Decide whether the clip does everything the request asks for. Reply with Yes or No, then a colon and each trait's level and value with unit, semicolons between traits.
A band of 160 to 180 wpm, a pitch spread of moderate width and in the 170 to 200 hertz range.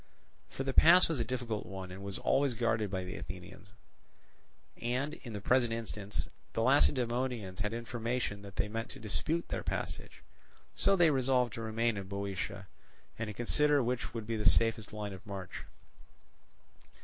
No: average, 170 wpm; average, 3.5 semitones; low, 115 Hz